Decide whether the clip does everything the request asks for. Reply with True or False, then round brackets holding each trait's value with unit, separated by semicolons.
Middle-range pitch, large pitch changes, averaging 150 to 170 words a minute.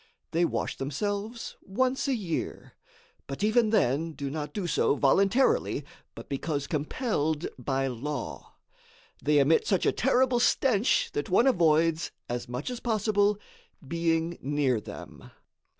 False (165 Hz; 7.0 semitones; 135 wpm)